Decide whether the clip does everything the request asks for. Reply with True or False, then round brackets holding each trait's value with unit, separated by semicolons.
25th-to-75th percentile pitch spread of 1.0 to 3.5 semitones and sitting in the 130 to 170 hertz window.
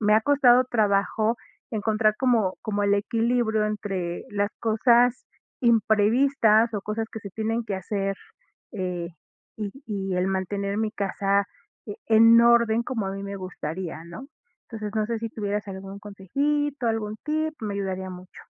False (2.7 semitones; 215 Hz)